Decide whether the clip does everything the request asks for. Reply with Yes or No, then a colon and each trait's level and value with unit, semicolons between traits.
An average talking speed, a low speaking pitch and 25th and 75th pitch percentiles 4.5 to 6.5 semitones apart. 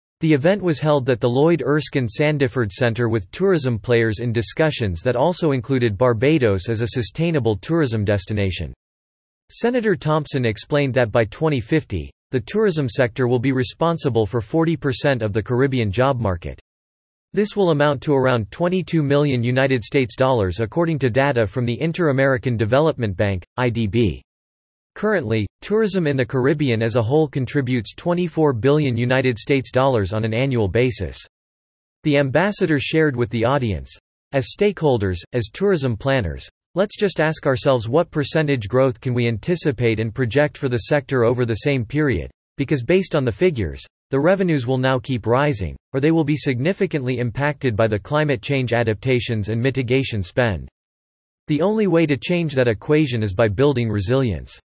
Yes: average, 160 wpm; low, 130 Hz; average, 5.0 semitones